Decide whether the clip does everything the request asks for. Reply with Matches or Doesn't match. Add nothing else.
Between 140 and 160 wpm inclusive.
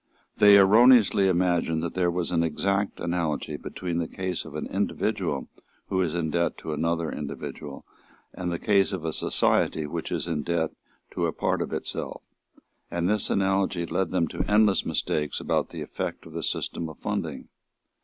Doesn't match